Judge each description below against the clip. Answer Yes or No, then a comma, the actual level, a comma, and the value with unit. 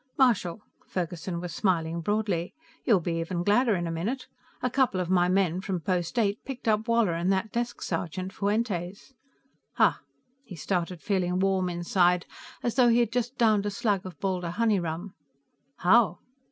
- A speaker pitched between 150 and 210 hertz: Yes, high, 190 Hz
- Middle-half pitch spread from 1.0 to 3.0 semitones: No, average, 3.9 semitones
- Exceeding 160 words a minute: Yes, average, 170 wpm